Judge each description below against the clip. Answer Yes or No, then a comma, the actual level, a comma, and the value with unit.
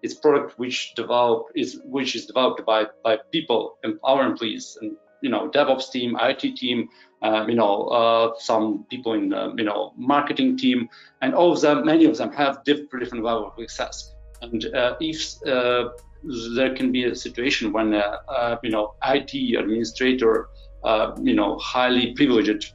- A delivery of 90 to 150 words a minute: No, average, 170 wpm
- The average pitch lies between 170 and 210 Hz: No, low, 125 Hz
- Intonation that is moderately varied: No, wide, 5.9 semitones